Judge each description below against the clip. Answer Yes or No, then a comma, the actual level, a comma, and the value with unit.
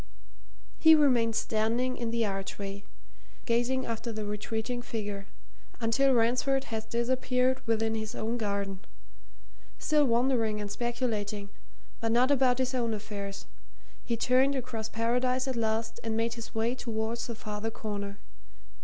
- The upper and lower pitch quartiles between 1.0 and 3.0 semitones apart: Yes, narrow, 2.5 semitones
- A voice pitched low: No, high, 230 Hz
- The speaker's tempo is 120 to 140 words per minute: Yes, slow, 135 wpm